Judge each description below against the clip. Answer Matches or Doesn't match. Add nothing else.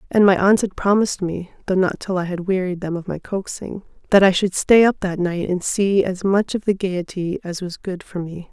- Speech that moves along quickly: Matches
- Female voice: Matches